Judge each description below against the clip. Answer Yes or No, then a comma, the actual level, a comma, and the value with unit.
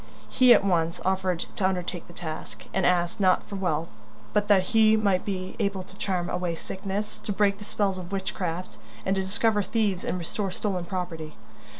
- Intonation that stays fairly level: Yes, narrow, 2.2 semitones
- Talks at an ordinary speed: Yes, average, 190 wpm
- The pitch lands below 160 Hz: No, high, 190 Hz